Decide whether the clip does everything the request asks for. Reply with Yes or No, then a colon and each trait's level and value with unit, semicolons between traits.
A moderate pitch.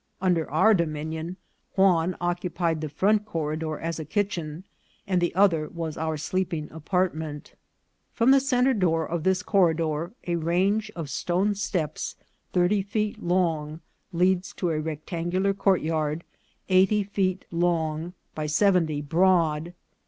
Yes: medium, 175 Hz